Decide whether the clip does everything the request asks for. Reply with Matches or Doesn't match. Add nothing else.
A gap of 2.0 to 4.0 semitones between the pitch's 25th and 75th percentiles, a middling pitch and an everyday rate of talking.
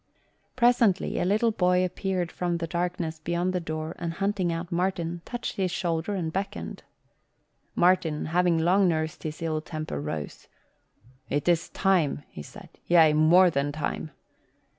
Matches